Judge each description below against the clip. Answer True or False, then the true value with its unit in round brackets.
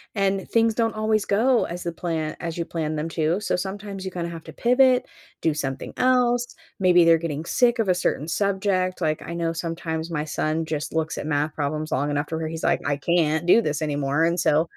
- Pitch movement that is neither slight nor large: True (4.0 semitones)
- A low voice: False (170 Hz)